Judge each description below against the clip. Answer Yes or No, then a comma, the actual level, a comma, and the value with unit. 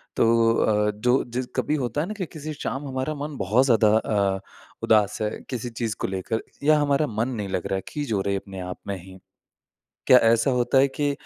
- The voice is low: Yes, low, 115 Hz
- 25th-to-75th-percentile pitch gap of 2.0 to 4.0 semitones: No, average, 5.0 semitones